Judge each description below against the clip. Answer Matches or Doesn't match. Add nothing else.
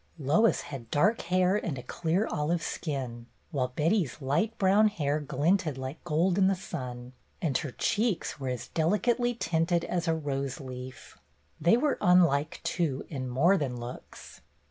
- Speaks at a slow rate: Doesn't match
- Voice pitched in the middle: Matches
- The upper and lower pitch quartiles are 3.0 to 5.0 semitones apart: Doesn't match